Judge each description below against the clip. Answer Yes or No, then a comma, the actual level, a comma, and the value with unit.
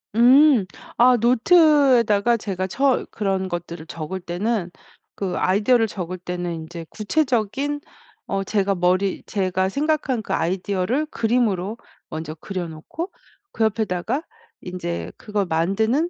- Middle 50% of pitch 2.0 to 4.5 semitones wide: No, average, 5.1 semitones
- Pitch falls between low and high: No, high, 200 Hz